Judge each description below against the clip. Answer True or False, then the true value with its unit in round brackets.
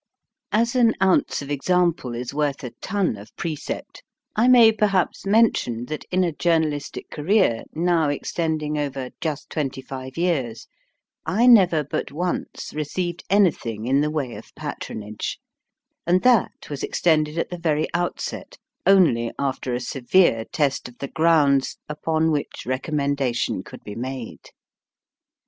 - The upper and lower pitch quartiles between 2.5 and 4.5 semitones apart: False (5.0 semitones)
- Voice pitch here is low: False (150 Hz)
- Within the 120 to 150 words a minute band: True (140 wpm)